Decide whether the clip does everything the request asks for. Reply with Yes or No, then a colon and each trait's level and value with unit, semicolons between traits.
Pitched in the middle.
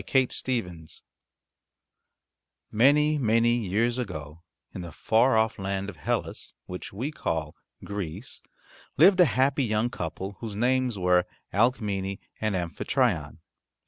No: low, 110 Hz